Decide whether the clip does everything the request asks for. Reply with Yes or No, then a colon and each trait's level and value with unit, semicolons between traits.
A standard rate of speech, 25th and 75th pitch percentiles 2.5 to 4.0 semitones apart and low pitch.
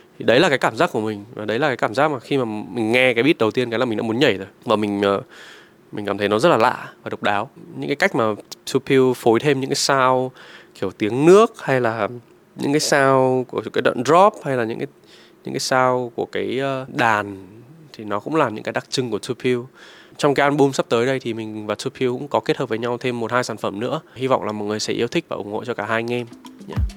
No: fast, 270 wpm; average, 3.7 semitones; low, 125 Hz